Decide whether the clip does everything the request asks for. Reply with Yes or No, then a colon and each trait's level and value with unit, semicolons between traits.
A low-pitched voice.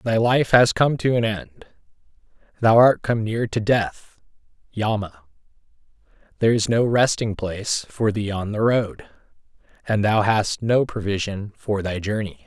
Yes: low, 110 Hz